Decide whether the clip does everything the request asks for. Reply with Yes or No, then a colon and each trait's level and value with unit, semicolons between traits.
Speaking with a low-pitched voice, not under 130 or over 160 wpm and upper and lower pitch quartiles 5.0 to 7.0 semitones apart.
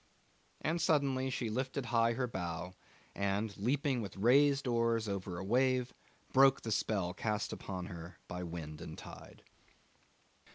Yes: low, 115 Hz; average, 150 wpm; wide, 5.5 semitones